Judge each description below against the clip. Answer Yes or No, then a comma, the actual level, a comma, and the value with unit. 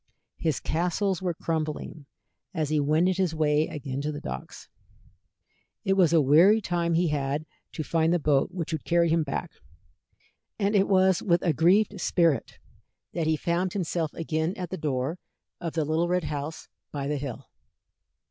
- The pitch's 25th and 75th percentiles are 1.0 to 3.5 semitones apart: Yes, average, 2.8 semitones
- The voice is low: No, medium, 165 Hz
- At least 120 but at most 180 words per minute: Yes, average, 170 wpm